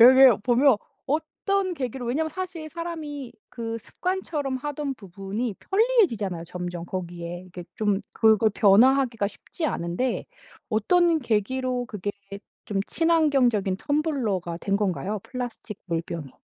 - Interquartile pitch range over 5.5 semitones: Yes, wide, 7.0 semitones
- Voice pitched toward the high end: Yes, high, 240 Hz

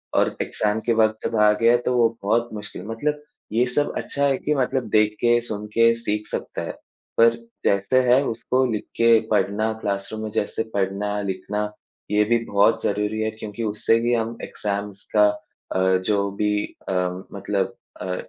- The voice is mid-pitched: No, low, 110 Hz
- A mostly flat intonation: Yes, narrow, 2.2 semitones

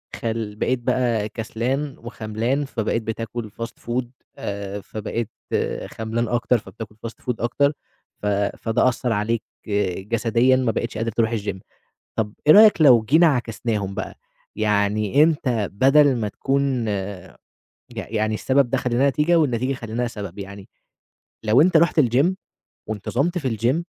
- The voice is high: No, low, 115 Hz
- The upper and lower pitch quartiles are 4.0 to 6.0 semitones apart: No, average, 3.4 semitones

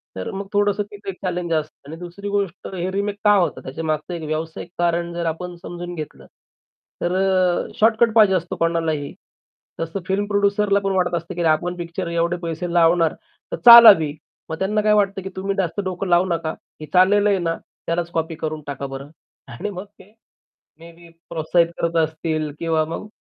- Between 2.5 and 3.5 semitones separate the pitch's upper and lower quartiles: Yes, average, 3.1 semitones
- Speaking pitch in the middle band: Yes, medium, 175 Hz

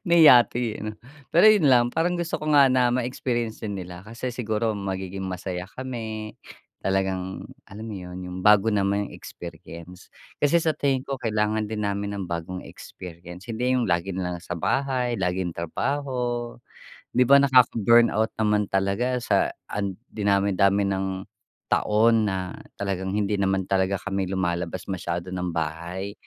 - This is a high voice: No, low, 100 Hz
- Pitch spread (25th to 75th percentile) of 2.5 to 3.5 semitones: No, average, 4.5 semitones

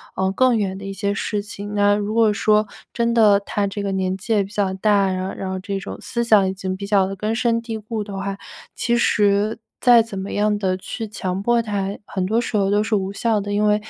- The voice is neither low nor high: No, high, 205 Hz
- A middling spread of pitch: No, narrow, 1.9 semitones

